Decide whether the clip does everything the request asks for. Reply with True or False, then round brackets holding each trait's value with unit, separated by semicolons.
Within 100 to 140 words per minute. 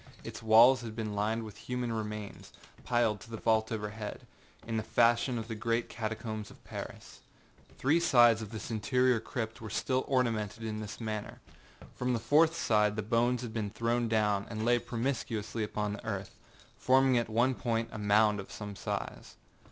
False (175 wpm)